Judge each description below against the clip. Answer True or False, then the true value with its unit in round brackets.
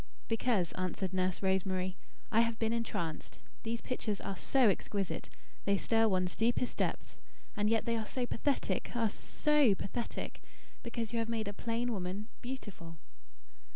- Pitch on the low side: False (220 Hz)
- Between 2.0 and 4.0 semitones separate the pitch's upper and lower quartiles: True (3.5 semitones)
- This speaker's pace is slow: False (155 wpm)